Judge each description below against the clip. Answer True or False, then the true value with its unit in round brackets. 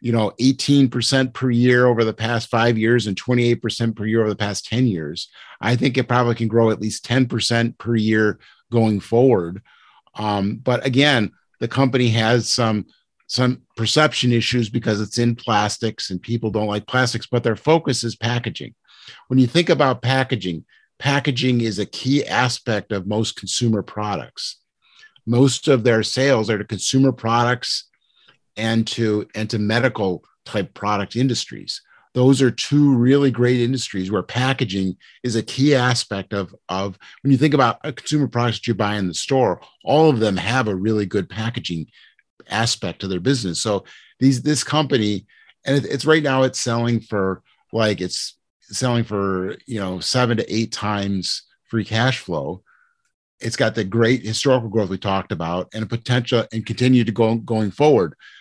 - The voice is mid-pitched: False (115 Hz)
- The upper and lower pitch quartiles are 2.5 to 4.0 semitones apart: True (3.2 semitones)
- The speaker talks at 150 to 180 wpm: True (175 wpm)